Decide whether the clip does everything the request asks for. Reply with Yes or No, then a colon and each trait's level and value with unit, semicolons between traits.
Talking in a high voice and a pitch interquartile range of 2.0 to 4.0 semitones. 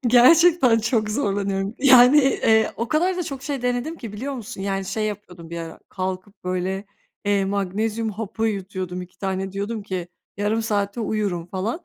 Yes: high, 210 Hz; average, 3.7 semitones